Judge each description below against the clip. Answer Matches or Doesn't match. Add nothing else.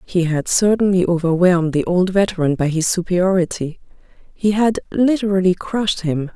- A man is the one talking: Doesn't match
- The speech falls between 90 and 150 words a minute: Matches